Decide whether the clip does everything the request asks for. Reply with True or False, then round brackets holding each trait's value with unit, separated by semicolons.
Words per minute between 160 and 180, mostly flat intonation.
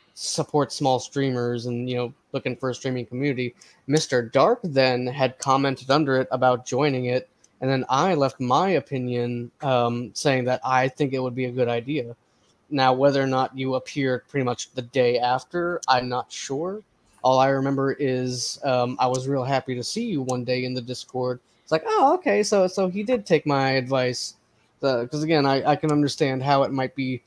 False (200 wpm; 1.9 semitones)